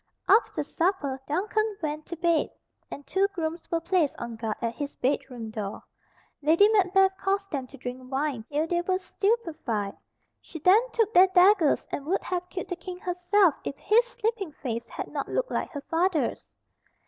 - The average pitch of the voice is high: Yes, very high, 340 Hz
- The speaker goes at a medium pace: Yes, average, 175 wpm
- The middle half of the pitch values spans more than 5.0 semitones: Yes, wide, 5.5 semitones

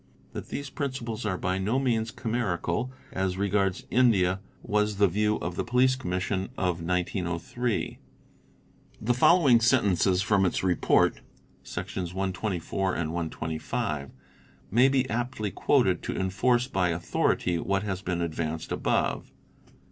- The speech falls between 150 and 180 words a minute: No, slow, 135 wpm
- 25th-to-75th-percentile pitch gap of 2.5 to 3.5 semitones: No, average, 4.8 semitones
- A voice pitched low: Yes, very low, 95 Hz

